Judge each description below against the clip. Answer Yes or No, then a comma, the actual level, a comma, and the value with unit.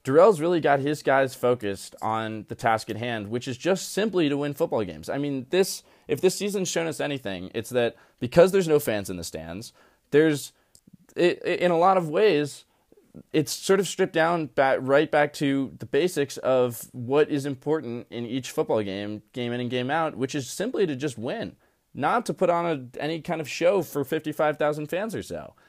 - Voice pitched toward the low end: No, medium, 145 Hz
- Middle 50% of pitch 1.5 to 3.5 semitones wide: No, average, 5.2 semitones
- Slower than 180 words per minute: No, fast, 205 wpm